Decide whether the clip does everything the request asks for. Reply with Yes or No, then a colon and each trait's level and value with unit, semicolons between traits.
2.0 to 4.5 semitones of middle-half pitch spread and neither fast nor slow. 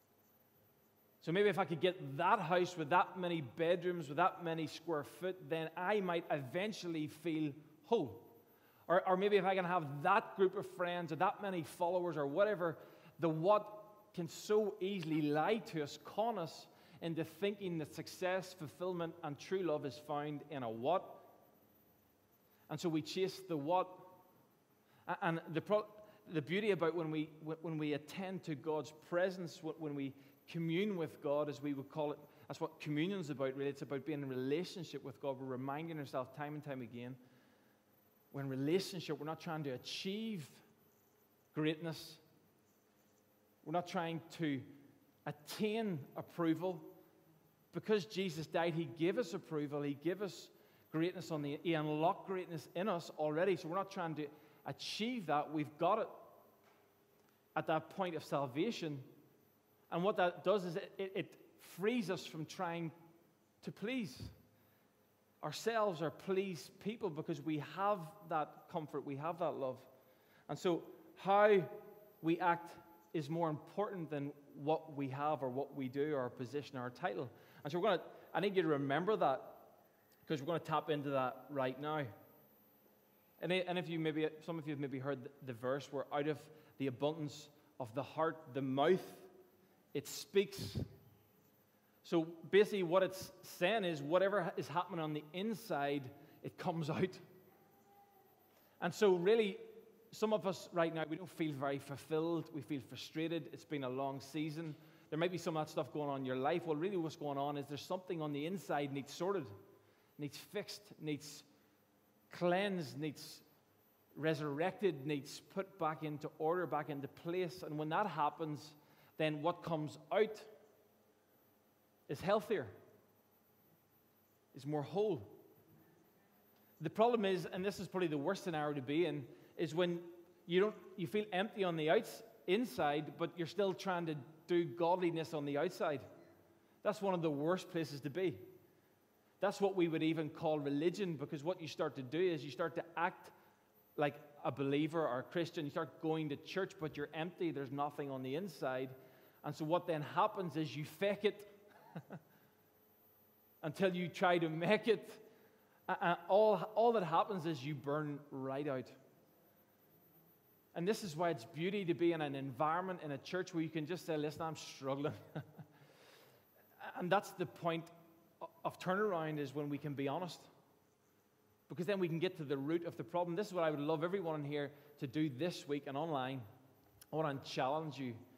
Yes: average, 4.1 semitones; average, 170 wpm